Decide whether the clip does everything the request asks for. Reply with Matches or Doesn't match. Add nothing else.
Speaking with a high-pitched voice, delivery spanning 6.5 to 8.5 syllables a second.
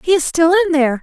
Matches